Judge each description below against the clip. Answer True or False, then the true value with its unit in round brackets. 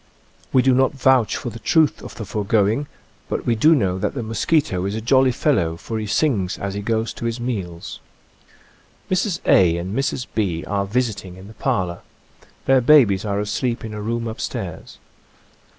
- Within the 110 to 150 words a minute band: False (185 wpm)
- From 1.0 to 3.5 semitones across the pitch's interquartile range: False (4.5 semitones)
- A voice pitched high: False (110 Hz)